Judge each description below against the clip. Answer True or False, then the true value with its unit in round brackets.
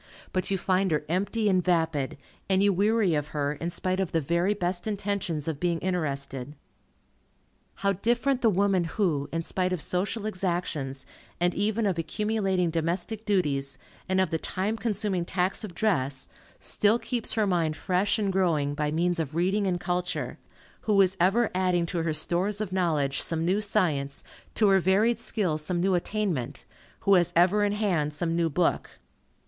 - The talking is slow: False (175 wpm)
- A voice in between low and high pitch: True (180 Hz)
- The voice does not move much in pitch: False (3.6 semitones)